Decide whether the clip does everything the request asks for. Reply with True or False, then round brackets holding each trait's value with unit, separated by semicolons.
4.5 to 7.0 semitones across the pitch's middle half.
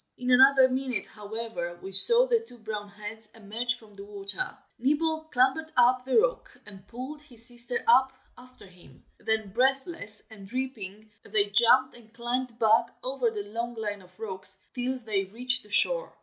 False (3.8 semitones)